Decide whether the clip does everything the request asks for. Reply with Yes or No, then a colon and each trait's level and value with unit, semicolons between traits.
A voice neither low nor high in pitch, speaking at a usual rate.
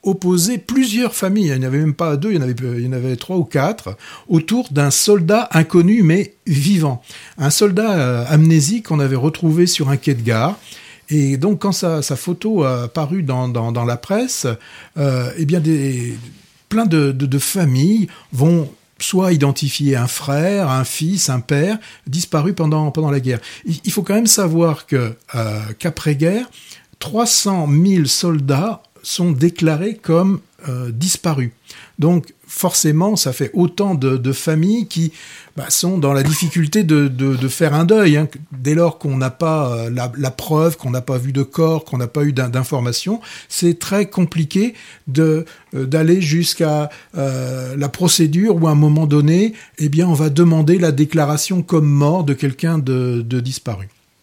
Yes: medium, 155 Hz; average, 180 wpm